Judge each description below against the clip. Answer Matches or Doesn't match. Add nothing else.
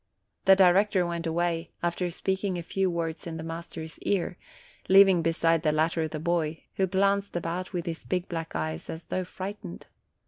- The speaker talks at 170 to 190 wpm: Matches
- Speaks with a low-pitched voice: Doesn't match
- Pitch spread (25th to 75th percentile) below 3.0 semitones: Matches